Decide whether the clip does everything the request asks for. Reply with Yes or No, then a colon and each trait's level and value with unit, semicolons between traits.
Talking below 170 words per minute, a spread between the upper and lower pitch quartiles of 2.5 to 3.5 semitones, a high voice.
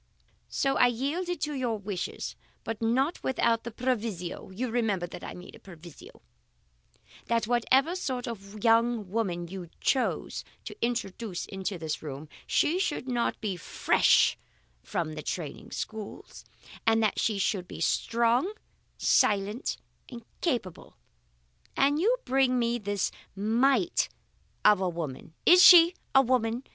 No: average, 140 wpm; average, 5.0 semitones; high, 230 Hz